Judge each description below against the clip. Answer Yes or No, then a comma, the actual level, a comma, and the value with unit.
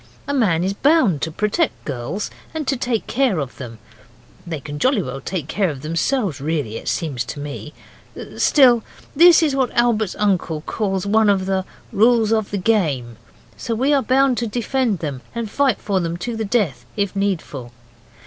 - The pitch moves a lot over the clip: Yes, wide, 7.3 semitones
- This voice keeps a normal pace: Yes, average, 180 wpm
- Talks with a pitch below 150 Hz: No, high, 200 Hz